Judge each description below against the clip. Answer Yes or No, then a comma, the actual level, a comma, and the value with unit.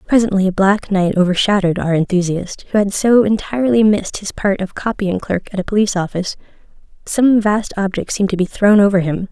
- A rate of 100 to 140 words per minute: No, average, 185 wpm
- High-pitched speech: Yes, high, 200 Hz